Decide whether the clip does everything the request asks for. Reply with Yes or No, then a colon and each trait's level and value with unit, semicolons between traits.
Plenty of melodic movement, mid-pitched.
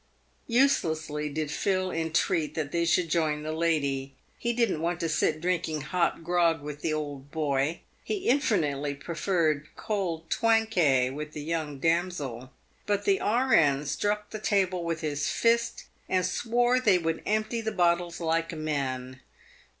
No: average, 4.2 semitones; medium, 165 Hz